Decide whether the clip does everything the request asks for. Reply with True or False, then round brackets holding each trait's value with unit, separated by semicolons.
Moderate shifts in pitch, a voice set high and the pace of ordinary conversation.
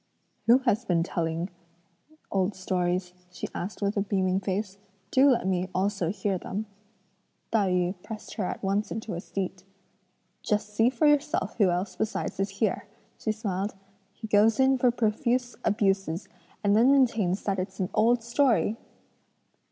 True (3.3 semitones; 205 Hz; 160 wpm)